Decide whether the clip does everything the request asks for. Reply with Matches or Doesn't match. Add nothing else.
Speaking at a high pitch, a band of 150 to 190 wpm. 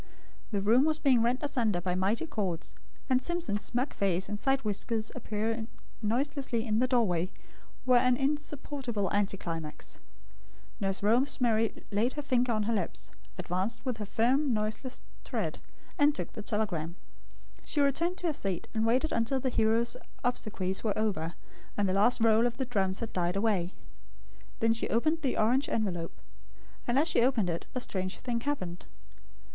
Matches